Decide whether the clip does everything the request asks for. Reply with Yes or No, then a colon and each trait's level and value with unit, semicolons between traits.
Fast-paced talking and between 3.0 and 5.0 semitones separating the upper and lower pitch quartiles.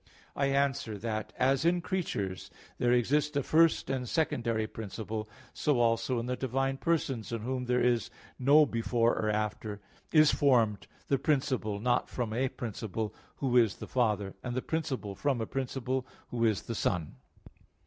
No: average, 170 wpm; average, 3.6 semitones